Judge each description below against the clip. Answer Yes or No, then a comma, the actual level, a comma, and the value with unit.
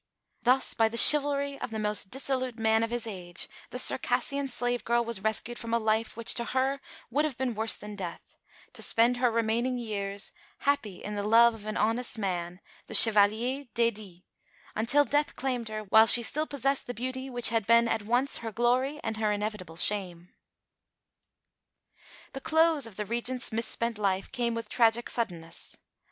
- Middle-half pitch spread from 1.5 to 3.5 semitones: Yes, average, 3.0 semitones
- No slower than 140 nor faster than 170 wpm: No, average, 180 wpm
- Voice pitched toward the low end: No, high, 230 Hz